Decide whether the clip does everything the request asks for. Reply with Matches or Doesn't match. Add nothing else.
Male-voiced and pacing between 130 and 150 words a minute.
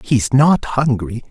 Matches